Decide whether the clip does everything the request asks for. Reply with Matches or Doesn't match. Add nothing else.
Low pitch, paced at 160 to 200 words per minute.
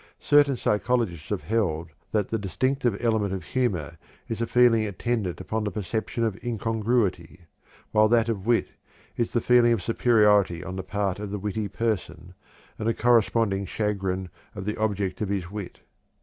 Matches